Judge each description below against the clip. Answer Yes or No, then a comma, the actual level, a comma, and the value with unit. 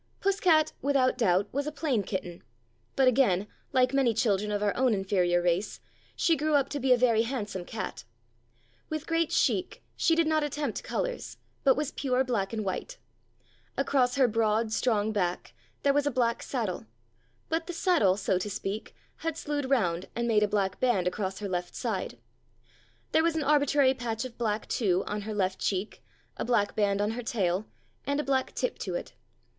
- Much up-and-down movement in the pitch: Yes, wide, 5.7 semitones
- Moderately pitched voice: No, high, 235 Hz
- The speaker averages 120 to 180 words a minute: No, average, 190 wpm